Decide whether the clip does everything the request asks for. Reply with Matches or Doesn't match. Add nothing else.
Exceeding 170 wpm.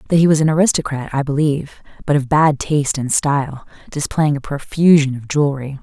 Matches